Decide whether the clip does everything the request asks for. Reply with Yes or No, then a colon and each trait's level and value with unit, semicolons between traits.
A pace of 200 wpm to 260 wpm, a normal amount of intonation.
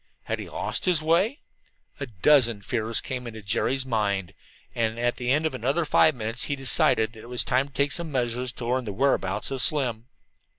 Yes: fast, 205 wpm; average, 3.8 semitones